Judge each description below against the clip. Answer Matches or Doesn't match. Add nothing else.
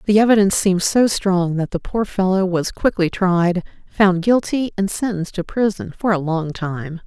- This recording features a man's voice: Doesn't match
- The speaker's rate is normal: Matches